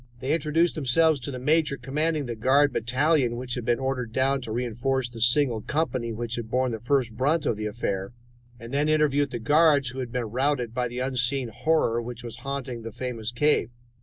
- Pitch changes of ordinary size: Yes, average, 3.3 semitones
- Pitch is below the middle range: Yes, low, 125 Hz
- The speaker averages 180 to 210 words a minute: Yes, fast, 205 wpm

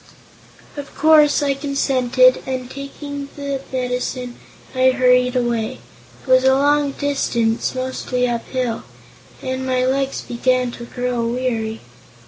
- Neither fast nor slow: No, slow, 125 wpm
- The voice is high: Yes, very high, 255 Hz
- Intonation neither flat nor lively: No, narrow, 1.8 semitones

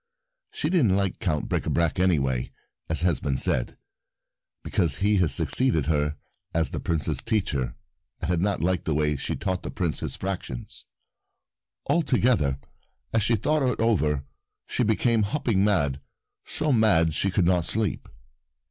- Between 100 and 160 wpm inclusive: Yes, average, 155 wpm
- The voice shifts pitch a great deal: Yes, wide, 6.2 semitones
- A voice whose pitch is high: No, very low, 90 Hz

